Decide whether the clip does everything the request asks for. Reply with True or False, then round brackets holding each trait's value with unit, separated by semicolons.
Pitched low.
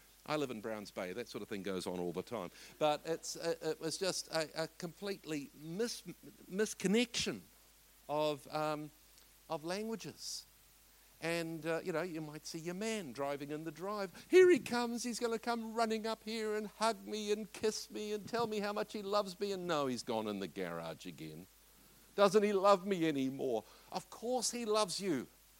False (180 Hz)